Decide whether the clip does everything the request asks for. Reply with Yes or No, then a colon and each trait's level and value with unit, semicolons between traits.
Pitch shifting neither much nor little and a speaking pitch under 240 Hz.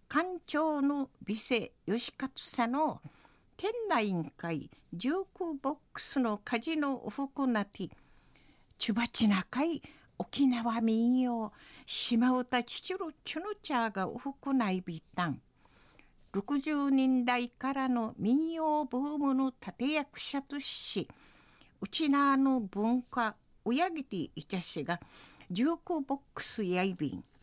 No: average, 4.9 semitones; very high, 255 Hz